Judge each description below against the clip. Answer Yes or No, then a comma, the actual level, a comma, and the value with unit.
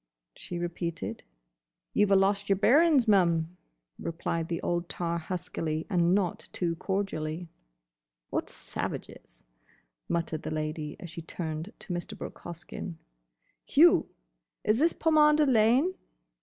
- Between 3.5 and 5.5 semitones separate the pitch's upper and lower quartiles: Yes, average, 3.8 semitones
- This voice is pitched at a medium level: Yes, medium, 175 Hz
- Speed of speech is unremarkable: No, slow, 130 wpm